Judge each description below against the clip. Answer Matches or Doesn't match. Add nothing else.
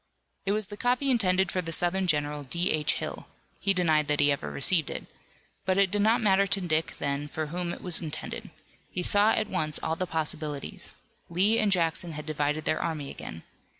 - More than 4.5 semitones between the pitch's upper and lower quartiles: Doesn't match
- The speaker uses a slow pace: Doesn't match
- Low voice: Doesn't match